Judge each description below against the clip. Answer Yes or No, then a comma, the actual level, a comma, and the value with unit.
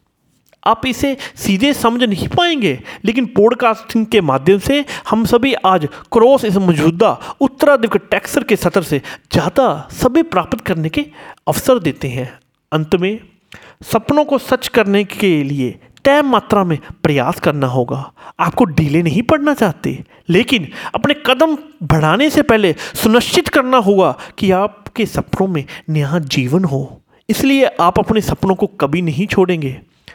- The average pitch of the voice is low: No, high, 205 Hz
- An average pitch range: No, wide, 7.7 semitones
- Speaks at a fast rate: No, average, 145 wpm